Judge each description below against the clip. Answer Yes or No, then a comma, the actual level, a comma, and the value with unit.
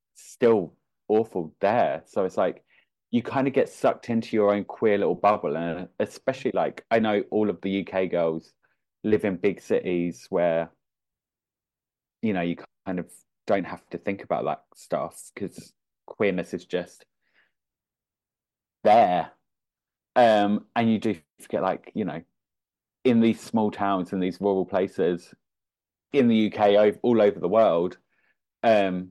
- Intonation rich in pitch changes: No, average, 2.9 semitones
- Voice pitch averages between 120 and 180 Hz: No, low, 100 Hz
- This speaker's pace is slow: No, average, 150 wpm